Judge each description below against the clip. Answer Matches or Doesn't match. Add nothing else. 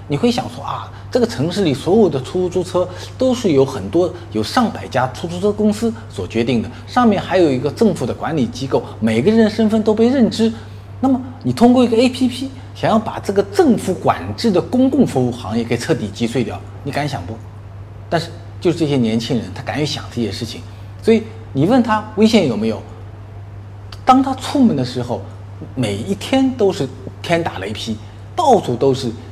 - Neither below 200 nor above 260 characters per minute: Doesn't match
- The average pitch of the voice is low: Matches